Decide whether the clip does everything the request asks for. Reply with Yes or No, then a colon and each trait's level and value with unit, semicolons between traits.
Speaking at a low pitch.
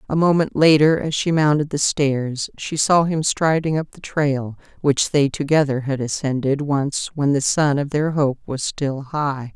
No: medium, 145 Hz